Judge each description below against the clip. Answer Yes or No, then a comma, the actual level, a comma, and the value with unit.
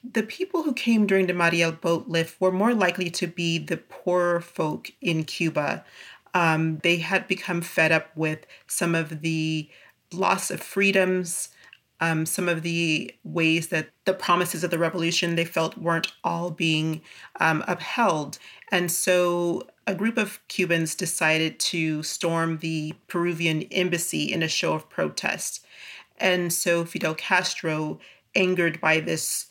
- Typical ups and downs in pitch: No, narrow, 2.1 semitones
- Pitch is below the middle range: No, medium, 170 Hz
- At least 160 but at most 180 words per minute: No, average, 150 wpm